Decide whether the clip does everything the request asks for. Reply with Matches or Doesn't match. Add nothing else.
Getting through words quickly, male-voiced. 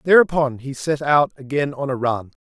Doesn't match